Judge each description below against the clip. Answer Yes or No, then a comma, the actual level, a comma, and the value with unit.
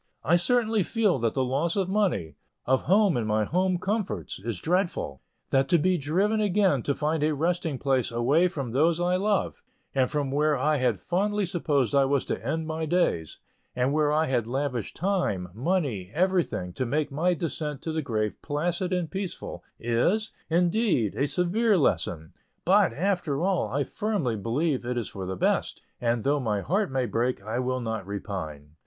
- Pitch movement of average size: No, wide, 6.8 semitones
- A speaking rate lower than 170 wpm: No, average, 185 wpm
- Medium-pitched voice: Yes, medium, 150 Hz